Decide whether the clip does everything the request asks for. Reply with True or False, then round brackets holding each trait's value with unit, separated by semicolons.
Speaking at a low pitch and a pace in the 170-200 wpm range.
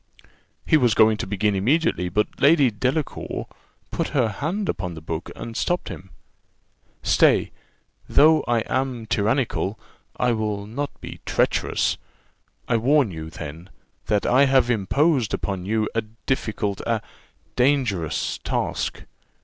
False (115 Hz; 135 wpm)